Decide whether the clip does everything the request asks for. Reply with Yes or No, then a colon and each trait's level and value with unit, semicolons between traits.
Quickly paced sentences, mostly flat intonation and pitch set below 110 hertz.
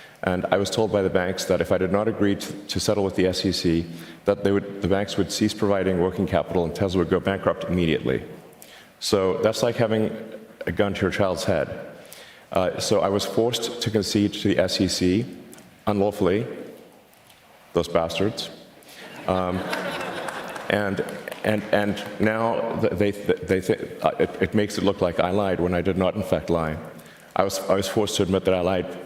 No: average, 190 wpm; narrow, 2.3 semitones; very low, 95 Hz